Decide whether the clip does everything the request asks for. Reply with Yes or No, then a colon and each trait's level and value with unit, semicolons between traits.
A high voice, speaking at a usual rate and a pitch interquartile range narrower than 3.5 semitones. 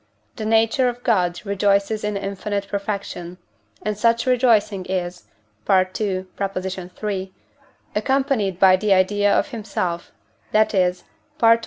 No: high, 200 Hz; slow, 125 wpm; average, 2.8 semitones